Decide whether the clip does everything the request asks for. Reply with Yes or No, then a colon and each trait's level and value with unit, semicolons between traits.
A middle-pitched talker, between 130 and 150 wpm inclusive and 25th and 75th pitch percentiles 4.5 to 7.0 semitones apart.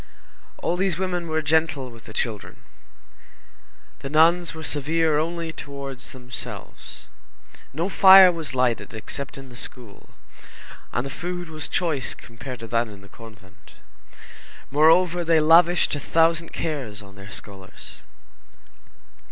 Yes: medium, 150 Hz; slow, 135 wpm; wide, 5.5 semitones